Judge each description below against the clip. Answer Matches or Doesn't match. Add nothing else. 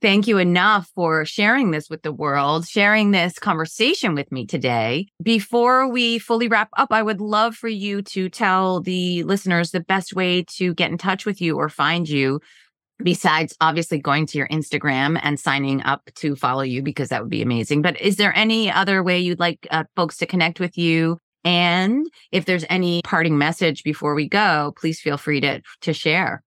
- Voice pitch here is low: Doesn't match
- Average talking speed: Matches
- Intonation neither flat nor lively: Matches